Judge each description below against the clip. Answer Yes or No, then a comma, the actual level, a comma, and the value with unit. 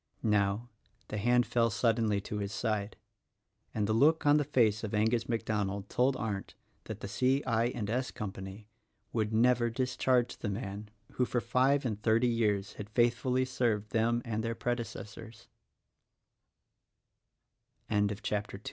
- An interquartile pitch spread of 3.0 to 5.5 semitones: No, narrow, 2.6 semitones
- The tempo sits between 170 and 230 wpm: No, average, 155 wpm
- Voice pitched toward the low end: Yes, low, 115 Hz